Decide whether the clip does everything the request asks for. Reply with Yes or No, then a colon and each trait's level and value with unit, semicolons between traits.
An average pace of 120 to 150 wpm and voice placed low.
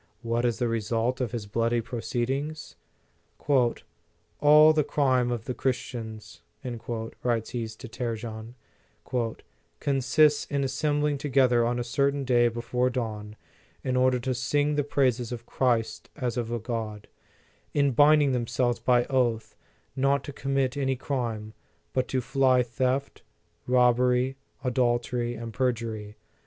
Yes: average, 140 wpm; low, 125 Hz